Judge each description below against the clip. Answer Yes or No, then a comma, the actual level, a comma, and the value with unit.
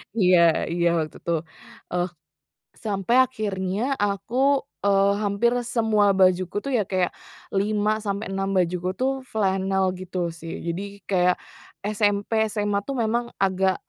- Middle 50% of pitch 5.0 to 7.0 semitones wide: No, narrow, 2.6 semitones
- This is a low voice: No, high, 200 Hz